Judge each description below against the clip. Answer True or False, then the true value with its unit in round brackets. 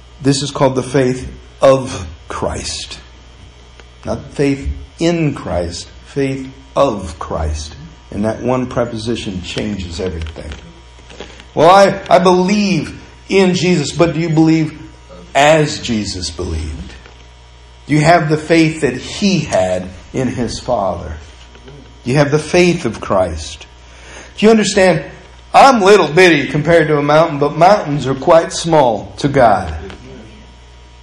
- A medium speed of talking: False (130 wpm)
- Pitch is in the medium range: False (125 Hz)